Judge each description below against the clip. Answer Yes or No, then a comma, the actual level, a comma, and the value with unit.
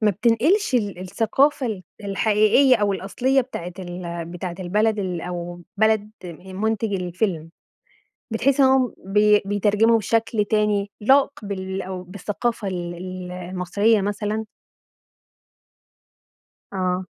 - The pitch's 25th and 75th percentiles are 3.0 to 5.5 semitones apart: Yes, average, 3.4 semitones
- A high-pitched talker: Yes, high, 205 Hz